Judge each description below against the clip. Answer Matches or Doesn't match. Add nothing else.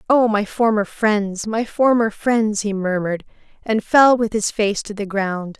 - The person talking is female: Matches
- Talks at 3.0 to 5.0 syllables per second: Matches